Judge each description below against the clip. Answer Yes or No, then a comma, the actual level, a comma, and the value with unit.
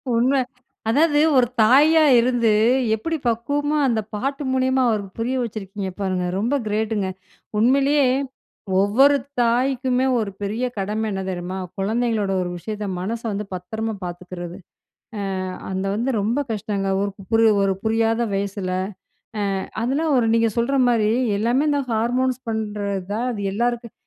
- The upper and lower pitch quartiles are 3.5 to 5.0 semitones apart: Yes, average, 4.0 semitones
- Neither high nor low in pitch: No, high, 225 Hz